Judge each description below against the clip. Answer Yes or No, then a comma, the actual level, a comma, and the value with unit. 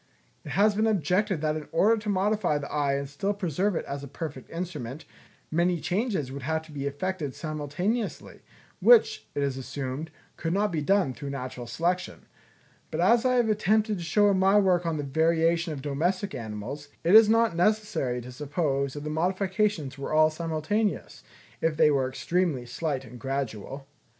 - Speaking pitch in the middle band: Yes, medium, 160 Hz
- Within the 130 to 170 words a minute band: No, average, 180 wpm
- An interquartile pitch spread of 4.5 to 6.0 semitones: Yes, wide, 5.6 semitones